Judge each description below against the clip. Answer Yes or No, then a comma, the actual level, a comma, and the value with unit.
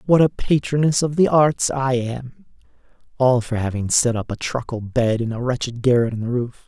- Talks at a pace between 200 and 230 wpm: Yes, fast, 205 wpm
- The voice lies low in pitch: Yes, low, 125 Hz